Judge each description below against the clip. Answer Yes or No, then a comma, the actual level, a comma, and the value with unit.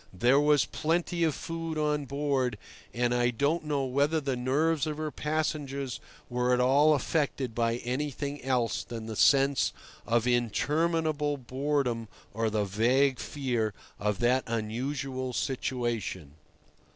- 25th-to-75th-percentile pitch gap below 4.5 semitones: Yes, average, 3.5 semitones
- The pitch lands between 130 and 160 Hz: Yes, low, 135 Hz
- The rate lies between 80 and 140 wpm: Yes, slow, 135 wpm